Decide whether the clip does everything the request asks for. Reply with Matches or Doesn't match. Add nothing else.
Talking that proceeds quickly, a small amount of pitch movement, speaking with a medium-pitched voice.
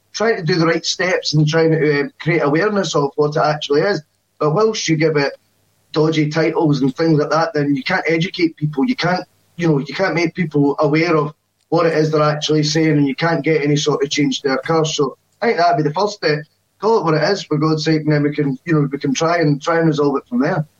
Matches